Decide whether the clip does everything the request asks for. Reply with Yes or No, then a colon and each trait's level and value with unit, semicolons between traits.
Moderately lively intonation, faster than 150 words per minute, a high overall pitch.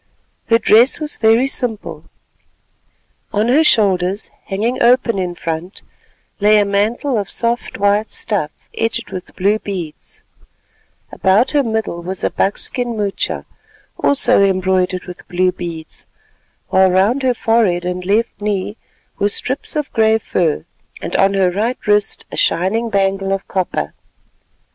No: average, 3.6 semitones; average, 140 wpm; high, 205 Hz